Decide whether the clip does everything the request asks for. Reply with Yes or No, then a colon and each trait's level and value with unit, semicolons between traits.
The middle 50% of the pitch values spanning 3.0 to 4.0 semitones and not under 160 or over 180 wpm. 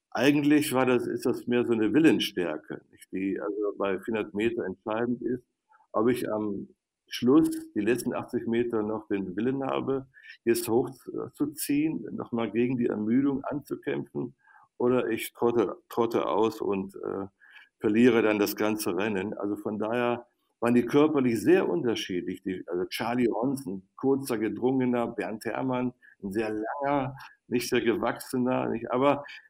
No: average, 3.7 semitones; average, 150 wpm